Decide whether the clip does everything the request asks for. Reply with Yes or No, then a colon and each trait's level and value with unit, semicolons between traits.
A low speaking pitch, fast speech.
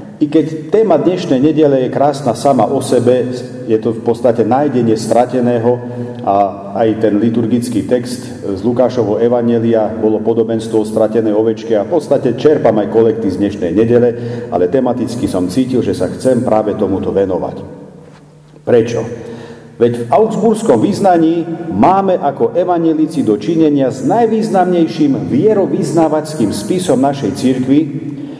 No: low, 125 Hz; average, 130 wpm